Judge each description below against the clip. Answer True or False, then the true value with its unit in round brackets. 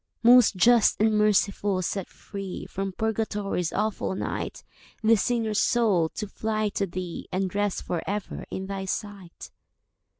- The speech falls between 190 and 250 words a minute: False (140 wpm)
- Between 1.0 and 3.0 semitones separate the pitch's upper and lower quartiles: True (2.4 semitones)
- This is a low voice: False (205 Hz)